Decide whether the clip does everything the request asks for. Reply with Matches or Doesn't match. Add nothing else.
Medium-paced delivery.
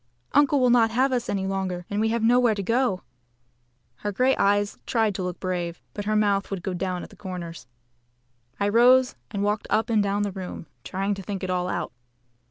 Doesn't match